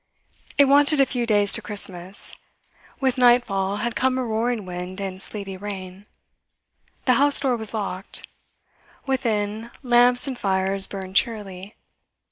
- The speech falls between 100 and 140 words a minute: Yes, slow, 135 wpm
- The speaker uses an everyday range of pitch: Yes, average, 4.2 semitones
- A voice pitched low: No, high, 215 Hz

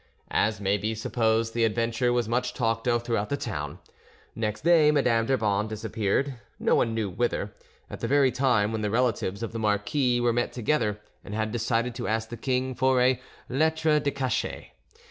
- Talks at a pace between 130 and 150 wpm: No, average, 185 wpm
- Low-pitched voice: Yes, low, 115 Hz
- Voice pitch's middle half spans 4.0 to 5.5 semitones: No, average, 2.8 semitones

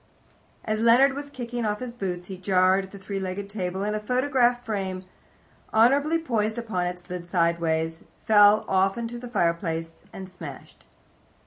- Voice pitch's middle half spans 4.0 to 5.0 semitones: Yes, average, 4.6 semitones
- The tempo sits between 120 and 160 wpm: Yes, average, 155 wpm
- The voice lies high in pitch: Yes, high, 200 Hz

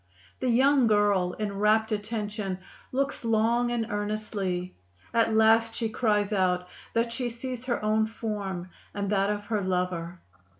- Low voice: No, high, 215 Hz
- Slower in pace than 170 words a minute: Yes, average, 145 wpm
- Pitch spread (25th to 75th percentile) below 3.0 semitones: Yes, narrow, 2.5 semitones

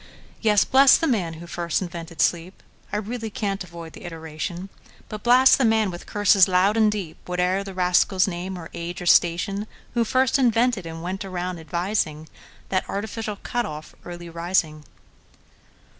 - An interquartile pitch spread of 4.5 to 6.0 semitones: No, average, 3.6 semitones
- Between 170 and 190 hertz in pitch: Yes, medium, 185 Hz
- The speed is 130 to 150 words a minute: Yes, average, 145 wpm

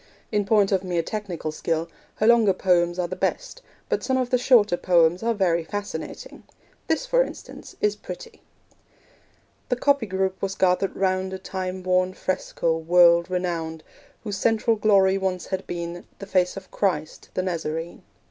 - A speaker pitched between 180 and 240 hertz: Yes, medium, 185 Hz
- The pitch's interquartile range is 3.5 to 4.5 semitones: No, average, 3.1 semitones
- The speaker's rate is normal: Yes, average, 165 wpm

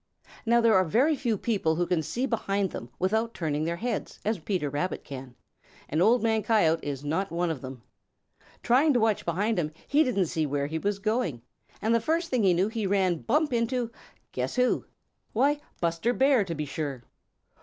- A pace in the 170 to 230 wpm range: Yes, average, 195 wpm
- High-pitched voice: Yes, high, 200 Hz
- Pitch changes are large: Yes, wide, 6.5 semitones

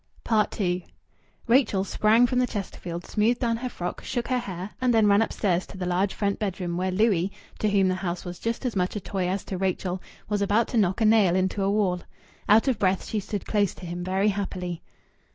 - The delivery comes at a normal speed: No, fast, 220 wpm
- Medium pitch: No, high, 195 Hz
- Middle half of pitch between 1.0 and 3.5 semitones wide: Yes, average, 3.1 semitones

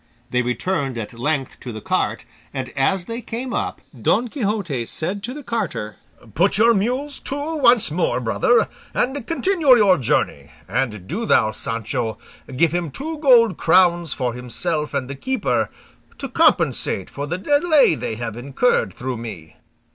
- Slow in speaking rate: No, average, 160 wpm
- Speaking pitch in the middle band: Yes, medium, 175 Hz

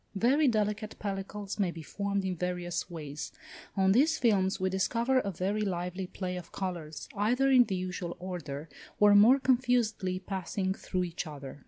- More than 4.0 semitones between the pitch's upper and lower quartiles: No, average, 3.1 semitones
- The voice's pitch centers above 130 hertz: Yes, high, 190 Hz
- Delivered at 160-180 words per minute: Yes, average, 165 wpm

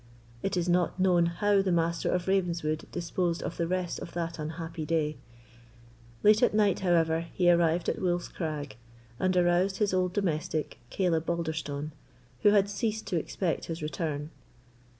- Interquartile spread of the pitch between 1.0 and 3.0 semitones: Yes, narrow, 2.4 semitones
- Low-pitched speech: No, medium, 175 Hz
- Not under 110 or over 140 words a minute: No, average, 160 wpm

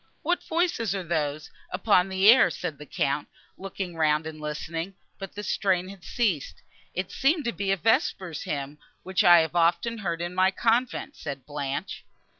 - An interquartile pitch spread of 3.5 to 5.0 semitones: Yes, average, 4.4 semitones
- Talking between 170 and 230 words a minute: Yes, average, 175 wpm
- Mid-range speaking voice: Yes, medium, 180 Hz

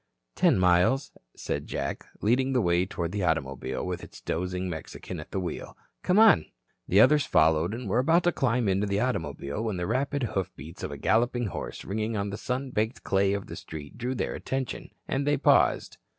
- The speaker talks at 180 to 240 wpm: Yes, average, 195 wpm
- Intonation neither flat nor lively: No, wide, 6.2 semitones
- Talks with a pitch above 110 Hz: No, low, 100 Hz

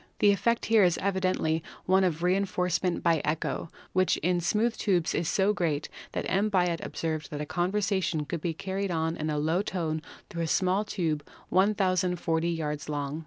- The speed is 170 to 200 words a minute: Yes, average, 175 wpm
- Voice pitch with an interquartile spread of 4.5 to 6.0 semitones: No, average, 3.1 semitones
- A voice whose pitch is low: No, medium, 175 Hz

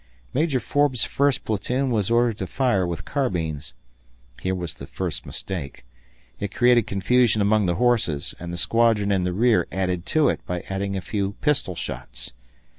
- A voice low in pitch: Yes, low, 100 Hz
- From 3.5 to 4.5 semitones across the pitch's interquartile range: No, average, 5.2 semitones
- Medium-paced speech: Yes, average, 170 wpm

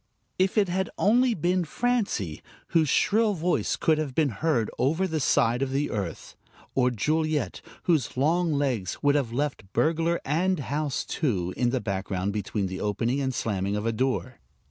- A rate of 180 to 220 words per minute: No, average, 170 wpm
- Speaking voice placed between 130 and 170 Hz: Yes, medium, 140 Hz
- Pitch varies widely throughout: Yes, wide, 6.5 semitones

